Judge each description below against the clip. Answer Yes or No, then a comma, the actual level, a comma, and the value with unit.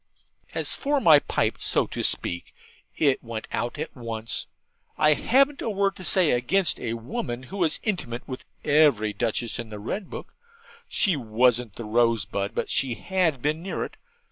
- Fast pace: No, average, 170 wpm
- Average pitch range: No, wide, 7.4 semitones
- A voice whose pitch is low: Yes, low, 130 Hz